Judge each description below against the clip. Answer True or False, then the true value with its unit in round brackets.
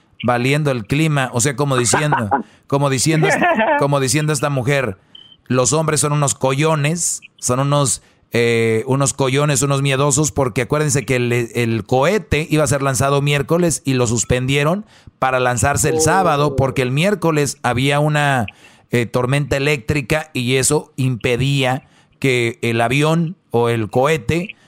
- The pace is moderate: True (145 wpm)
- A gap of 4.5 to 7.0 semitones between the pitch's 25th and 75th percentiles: False (3.0 semitones)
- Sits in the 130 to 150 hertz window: True (140 Hz)